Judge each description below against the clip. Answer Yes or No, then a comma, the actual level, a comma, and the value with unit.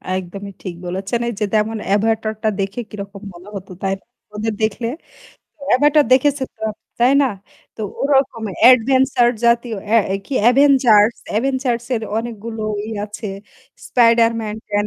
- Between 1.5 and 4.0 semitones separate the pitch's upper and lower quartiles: Yes, average, 3.1 semitones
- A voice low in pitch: No, high, 225 Hz